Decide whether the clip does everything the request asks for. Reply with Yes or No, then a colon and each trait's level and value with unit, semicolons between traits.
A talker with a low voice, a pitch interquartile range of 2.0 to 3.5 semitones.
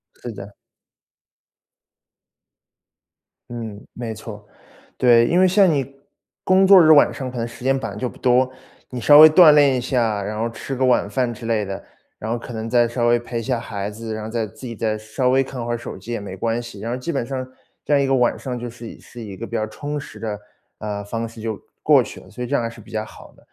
Yes: low, 120 Hz; average, 2.8 semitones